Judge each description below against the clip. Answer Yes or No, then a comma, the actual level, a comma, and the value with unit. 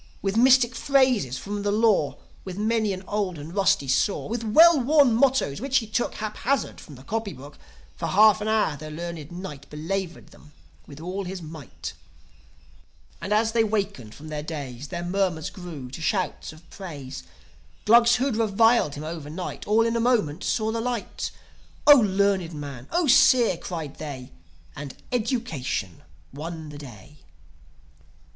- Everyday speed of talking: Yes, average, 160 wpm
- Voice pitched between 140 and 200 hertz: Yes, high, 190 Hz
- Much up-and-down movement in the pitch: Yes, wide, 6.9 semitones